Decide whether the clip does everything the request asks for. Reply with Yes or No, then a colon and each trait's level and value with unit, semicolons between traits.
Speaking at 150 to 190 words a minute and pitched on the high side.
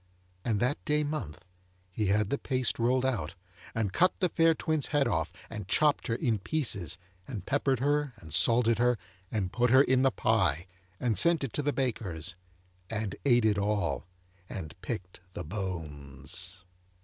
No: average, 170 wpm; low, 110 Hz